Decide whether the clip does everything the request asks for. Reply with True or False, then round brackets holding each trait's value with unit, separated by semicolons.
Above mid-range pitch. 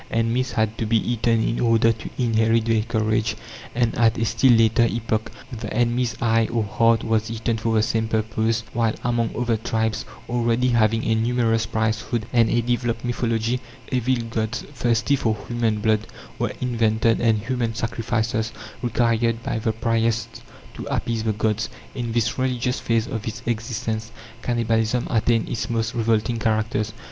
False (115 Hz)